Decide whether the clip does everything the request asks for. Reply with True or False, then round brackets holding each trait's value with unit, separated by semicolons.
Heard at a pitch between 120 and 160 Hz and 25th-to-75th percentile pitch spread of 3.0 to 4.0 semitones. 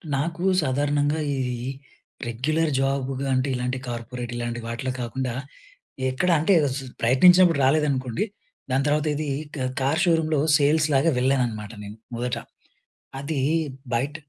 True (135 Hz; 3.4 semitones)